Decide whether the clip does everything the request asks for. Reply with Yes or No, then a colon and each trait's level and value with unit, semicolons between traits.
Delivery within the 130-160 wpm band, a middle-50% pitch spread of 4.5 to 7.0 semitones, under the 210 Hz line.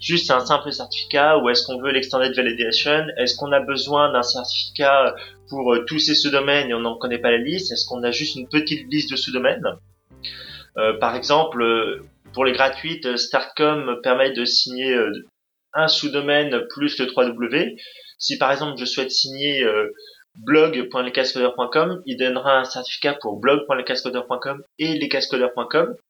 No: average, 150 wpm; average, 3.1 semitones; low, 135 Hz